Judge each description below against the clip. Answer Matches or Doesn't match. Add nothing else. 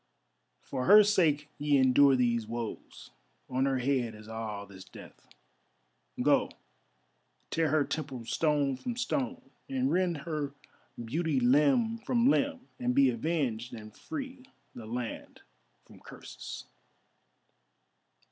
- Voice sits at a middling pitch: Matches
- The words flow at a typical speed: Doesn't match